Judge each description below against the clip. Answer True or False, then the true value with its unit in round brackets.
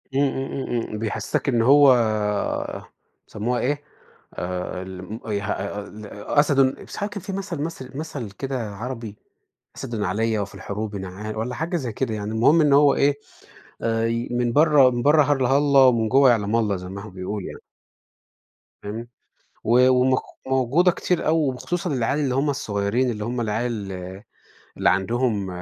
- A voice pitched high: False (120 Hz)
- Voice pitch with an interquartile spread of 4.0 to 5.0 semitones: True (4.7 semitones)